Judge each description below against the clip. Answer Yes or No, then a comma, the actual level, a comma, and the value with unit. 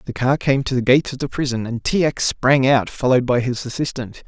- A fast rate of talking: Yes, fast, 255 wpm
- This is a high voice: No, low, 130 Hz